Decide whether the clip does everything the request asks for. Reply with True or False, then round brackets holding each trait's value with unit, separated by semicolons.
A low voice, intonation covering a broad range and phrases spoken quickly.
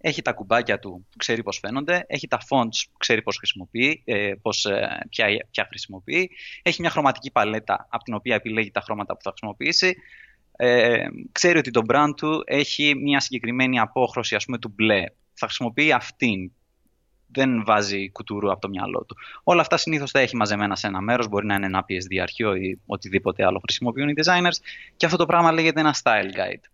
True (120 Hz; 6.2 semitones; 190 wpm)